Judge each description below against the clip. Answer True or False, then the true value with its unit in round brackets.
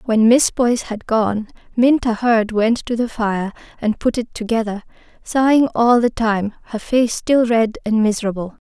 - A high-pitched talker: True (230 Hz)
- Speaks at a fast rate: False (175 wpm)